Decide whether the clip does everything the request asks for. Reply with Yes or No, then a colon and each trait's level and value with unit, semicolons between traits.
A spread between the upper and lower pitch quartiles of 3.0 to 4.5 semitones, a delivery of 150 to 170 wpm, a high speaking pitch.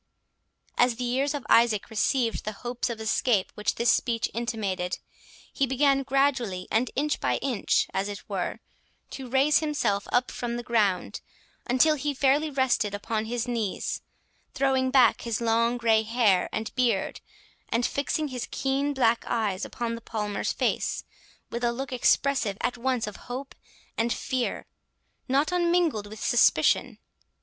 Yes: average, 3.3 semitones; average, 155 wpm; high, 240 Hz